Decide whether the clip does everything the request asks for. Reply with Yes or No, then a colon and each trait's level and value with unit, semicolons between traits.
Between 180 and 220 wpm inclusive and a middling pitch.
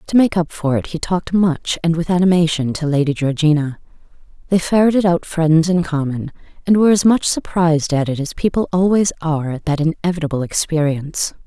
Yes: average, 185 wpm; medium, 165 Hz